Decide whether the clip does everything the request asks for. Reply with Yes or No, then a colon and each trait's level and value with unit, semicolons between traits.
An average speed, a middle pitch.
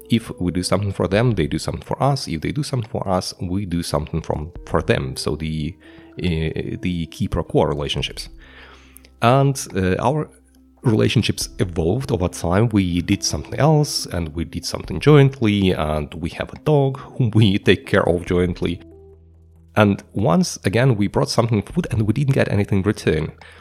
No: average, 180 wpm; very low, 95 Hz